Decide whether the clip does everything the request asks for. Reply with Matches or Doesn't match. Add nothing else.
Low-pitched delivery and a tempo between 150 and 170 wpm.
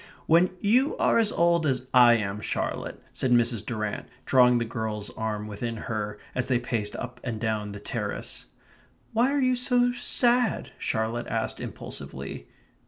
Matches